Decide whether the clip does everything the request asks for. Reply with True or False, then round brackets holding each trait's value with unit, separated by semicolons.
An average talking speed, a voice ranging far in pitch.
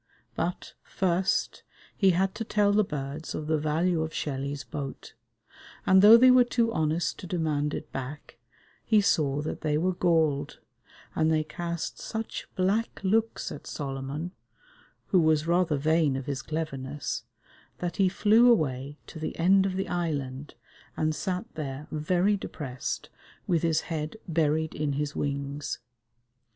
False (150 wpm; 4.0 semitones)